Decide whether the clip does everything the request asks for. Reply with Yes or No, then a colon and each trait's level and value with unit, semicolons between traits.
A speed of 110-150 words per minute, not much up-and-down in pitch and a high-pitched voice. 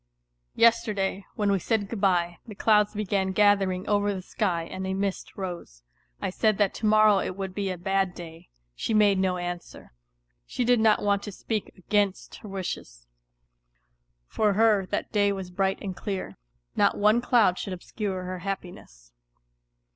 No: average, 170 wpm; narrow, 2.2 semitones; high, 195 Hz